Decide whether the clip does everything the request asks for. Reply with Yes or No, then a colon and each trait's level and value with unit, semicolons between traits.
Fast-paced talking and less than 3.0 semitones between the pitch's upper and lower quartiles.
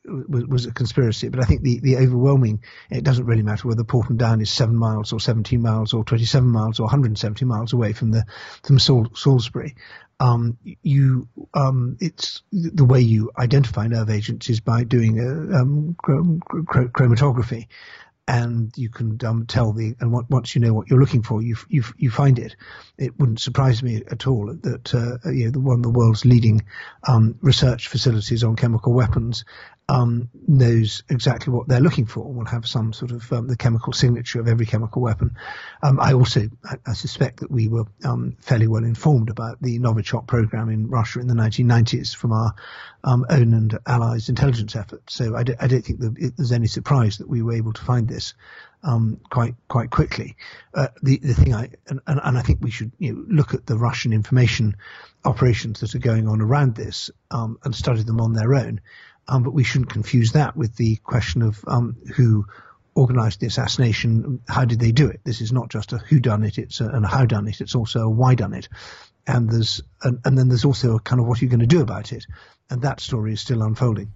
Yes: fast, 215 wpm; narrow, 2.5 semitones